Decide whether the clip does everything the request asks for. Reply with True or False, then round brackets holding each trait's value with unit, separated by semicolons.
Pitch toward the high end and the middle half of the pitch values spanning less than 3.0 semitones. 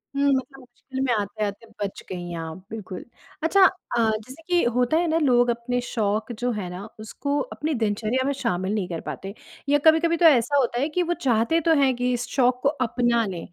False (245 Hz; 4.8 semitones)